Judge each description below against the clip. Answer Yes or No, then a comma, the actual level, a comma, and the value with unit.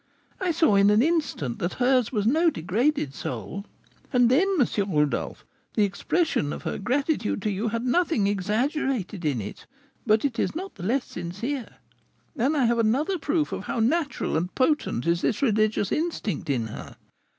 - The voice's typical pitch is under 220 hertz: No, high, 230 Hz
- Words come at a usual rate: Yes, average, 175 wpm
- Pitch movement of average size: No, wide, 7.0 semitones